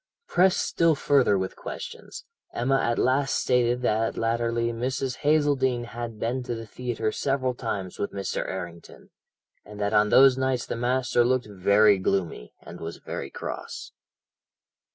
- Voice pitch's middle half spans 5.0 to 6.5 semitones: No, average, 3.8 semitones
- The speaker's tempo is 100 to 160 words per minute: Yes, average, 150 wpm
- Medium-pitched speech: No, low, 120 Hz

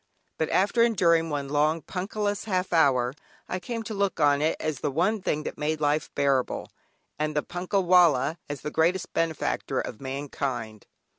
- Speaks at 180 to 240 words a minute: No, average, 170 wpm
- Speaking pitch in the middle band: Yes, medium, 160 Hz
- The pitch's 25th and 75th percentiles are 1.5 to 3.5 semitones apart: No, average, 4.3 semitones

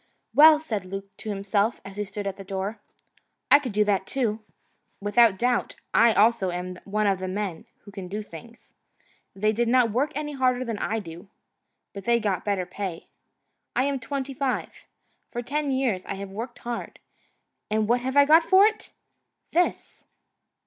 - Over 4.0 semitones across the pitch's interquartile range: Yes, average, 4.4 semitones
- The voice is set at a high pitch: Yes, high, 215 Hz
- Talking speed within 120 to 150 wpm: No, average, 180 wpm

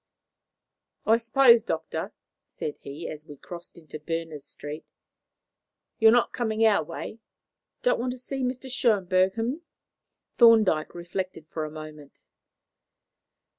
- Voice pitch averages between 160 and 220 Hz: Yes, medium, 185 Hz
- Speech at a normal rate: No, slow, 130 wpm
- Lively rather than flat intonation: Yes, wide, 7.0 semitones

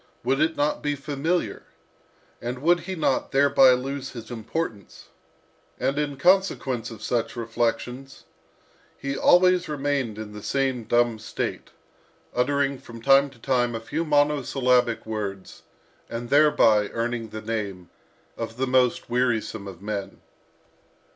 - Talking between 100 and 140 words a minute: Yes, slow, 135 wpm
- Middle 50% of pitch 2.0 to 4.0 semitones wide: Yes, average, 3.7 semitones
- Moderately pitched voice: No, low, 125 Hz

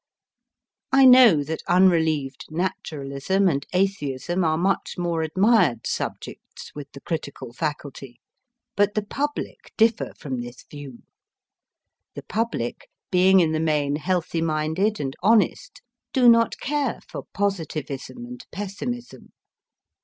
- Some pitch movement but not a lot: No, wide, 6.1 semitones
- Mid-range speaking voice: Yes, medium, 170 Hz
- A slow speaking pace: Yes, slow, 120 wpm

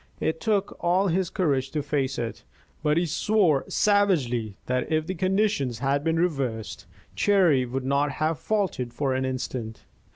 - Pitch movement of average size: No, wide, 5.9 semitones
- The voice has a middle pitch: Yes, medium, 150 Hz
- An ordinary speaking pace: Yes, average, 160 wpm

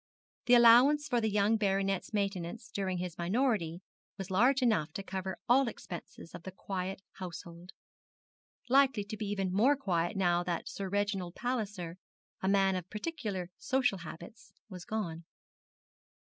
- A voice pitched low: No, high, 195 Hz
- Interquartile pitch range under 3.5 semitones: No, average, 3.8 semitones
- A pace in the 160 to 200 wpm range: No, average, 150 wpm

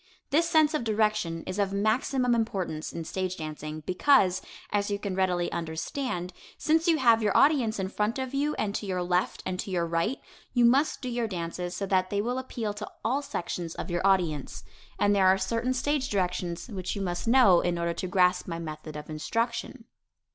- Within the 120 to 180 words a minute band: No, average, 200 wpm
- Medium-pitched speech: No, high, 195 Hz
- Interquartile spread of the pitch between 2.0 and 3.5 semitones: No, average, 5.2 semitones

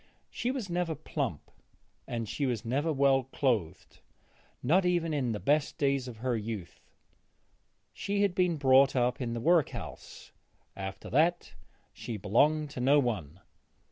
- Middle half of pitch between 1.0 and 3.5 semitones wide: No, average, 5.1 semitones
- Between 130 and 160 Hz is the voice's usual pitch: Yes, low, 135 Hz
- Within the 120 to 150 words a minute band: Yes, average, 145 wpm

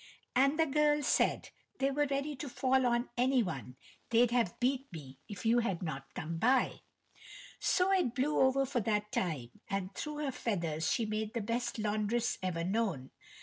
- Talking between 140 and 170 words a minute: No, average, 180 wpm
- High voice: Yes, high, 235 Hz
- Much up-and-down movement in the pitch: Yes, wide, 6.3 semitones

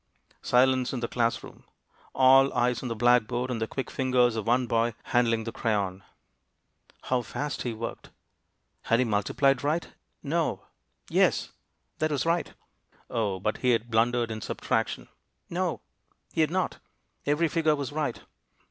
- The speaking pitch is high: No, low, 125 Hz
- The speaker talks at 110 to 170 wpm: Yes, average, 155 wpm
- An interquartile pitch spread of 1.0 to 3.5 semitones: Yes, average, 3.2 semitones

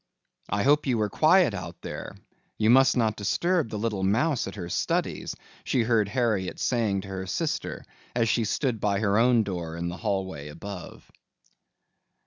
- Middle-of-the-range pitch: No, low, 105 Hz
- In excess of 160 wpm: Yes, average, 170 wpm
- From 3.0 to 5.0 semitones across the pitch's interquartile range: Yes, average, 4.0 semitones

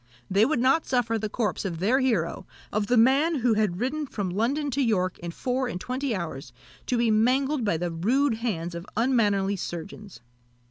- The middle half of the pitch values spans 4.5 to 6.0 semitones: Yes, average, 5.3 semitones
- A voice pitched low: No, high, 225 Hz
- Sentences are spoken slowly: No, average, 190 wpm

